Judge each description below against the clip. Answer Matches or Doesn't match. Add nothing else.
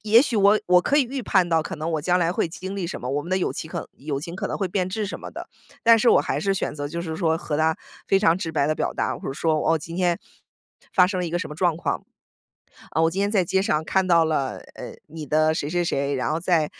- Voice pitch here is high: Doesn't match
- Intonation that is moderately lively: Matches